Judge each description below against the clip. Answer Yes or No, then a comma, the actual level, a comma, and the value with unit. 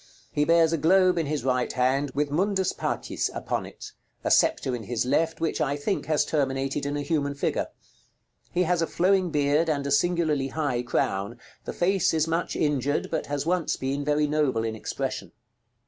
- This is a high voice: No, medium, 150 Hz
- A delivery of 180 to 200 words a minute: Yes, average, 190 wpm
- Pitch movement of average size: Yes, average, 3.2 semitones